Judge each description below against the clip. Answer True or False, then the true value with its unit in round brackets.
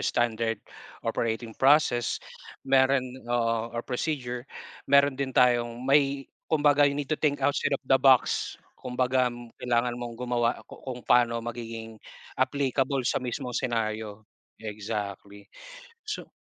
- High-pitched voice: False (125 Hz)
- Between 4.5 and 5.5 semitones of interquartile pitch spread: False (2.7 semitones)